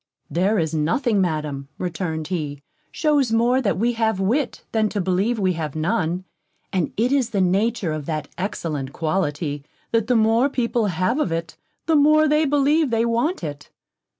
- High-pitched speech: Yes, high, 195 Hz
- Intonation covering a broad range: Yes, wide, 6.8 semitones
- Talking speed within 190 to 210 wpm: No, average, 175 wpm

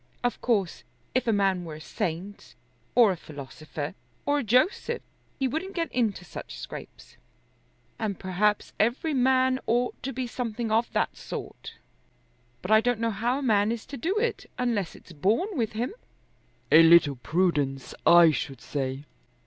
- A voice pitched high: Yes, high, 220 Hz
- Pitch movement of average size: No, wide, 6.4 semitones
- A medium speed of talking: Yes, average, 165 wpm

